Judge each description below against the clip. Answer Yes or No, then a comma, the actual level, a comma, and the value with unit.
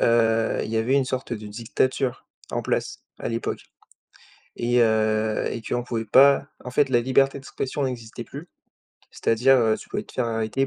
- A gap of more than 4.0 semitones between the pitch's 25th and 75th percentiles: No, average, 2.8 semitones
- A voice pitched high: No, low, 120 Hz